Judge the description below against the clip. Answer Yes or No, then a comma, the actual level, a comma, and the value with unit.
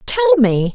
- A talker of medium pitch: No, very high, 280 Hz